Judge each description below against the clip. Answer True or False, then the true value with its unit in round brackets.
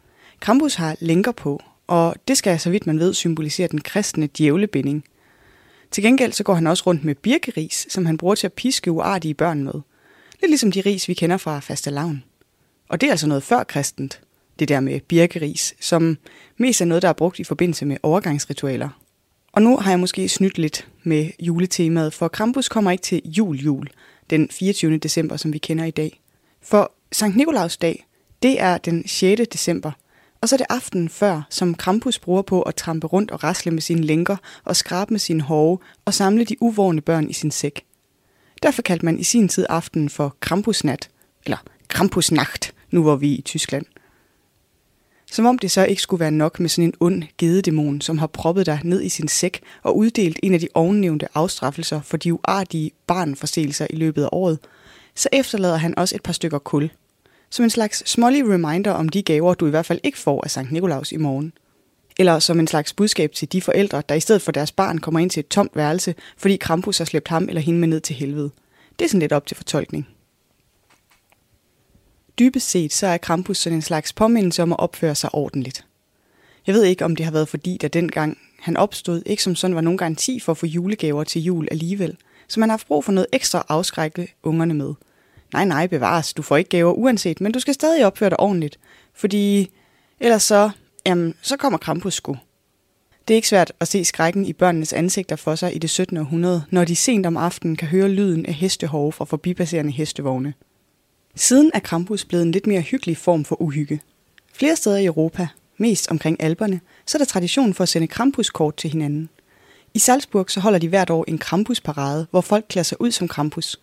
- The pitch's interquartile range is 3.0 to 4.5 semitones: True (3.9 semitones)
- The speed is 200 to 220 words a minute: True (205 wpm)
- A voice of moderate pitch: True (170 Hz)